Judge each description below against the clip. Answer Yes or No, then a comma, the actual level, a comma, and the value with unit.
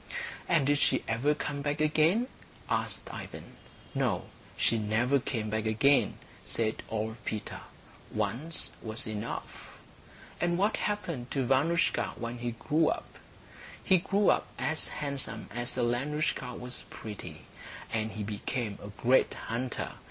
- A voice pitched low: Yes, low, 125 Hz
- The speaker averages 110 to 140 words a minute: Yes, slow, 135 wpm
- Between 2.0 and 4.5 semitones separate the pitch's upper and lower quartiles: No, average, 5.3 semitones